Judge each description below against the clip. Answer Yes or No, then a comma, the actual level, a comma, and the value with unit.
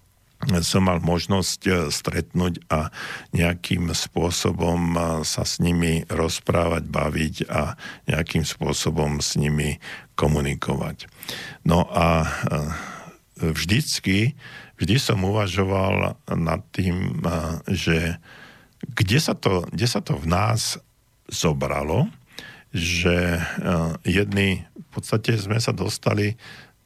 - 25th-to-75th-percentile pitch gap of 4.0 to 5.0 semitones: Yes, average, 4.3 semitones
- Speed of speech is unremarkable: No, slow, 95 wpm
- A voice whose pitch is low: Yes, very low, 90 Hz